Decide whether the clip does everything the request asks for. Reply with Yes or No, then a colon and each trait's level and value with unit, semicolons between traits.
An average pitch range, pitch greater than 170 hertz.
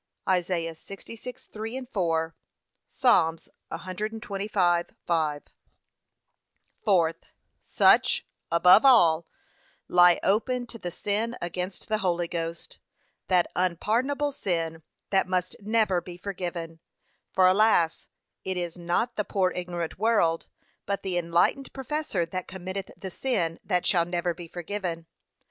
Yes: average, 3.6 semitones; medium, 185 Hz